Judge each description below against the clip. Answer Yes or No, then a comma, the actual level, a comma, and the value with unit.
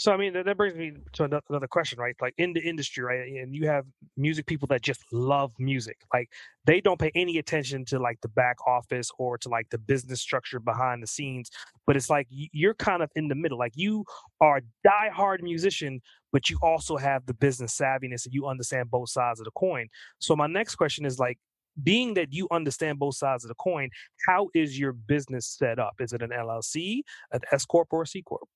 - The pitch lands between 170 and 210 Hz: No, medium, 140 Hz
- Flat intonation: No, average, 4.5 semitones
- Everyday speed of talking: No, fast, 225 wpm